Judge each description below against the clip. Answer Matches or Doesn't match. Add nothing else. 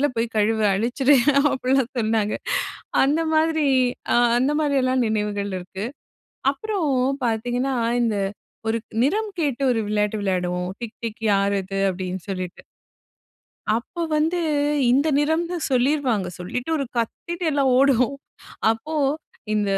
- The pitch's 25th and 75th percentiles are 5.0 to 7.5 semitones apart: Matches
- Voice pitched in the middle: Doesn't match